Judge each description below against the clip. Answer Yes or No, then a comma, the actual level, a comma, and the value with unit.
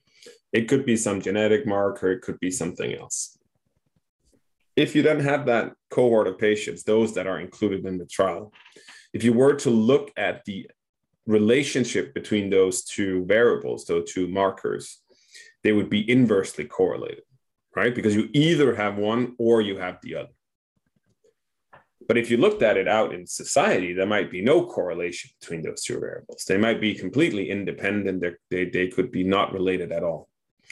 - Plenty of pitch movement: Yes, wide, 7.9 semitones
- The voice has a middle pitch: No, low, 110 Hz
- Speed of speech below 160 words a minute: No, average, 170 wpm